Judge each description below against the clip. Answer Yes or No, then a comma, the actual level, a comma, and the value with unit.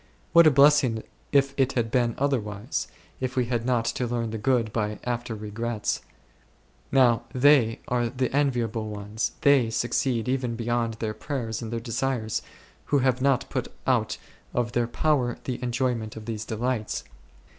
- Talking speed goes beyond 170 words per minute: No, average, 160 wpm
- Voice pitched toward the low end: Yes, low, 120 Hz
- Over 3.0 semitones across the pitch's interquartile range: No, narrow, 2.5 semitones